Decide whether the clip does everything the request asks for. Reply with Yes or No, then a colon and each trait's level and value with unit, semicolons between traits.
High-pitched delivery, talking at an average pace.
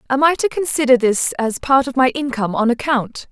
No: very high, 255 Hz; fast, 215 wpm